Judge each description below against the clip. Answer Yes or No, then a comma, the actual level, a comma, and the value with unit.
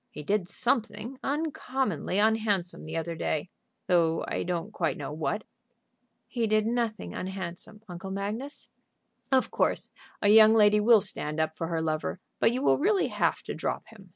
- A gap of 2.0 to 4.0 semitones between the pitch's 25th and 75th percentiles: No, average, 4.8 semitones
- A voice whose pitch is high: Yes, high, 205 Hz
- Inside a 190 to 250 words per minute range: No, average, 165 wpm